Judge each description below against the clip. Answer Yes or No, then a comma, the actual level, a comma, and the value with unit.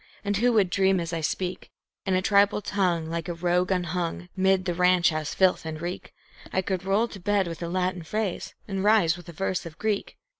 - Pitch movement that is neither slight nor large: No, narrow, 2.3 semitones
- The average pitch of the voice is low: No, medium, 185 Hz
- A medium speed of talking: No, fast, 220 wpm